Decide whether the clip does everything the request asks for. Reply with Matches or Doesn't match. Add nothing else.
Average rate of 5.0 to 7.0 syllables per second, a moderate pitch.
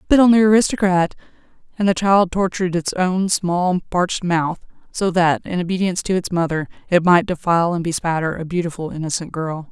Matches